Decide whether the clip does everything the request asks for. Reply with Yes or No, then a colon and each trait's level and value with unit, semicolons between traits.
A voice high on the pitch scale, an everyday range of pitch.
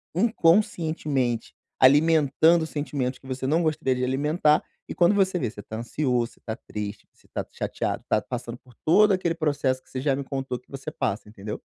No: medium, 140 Hz; average, 4.2 semitones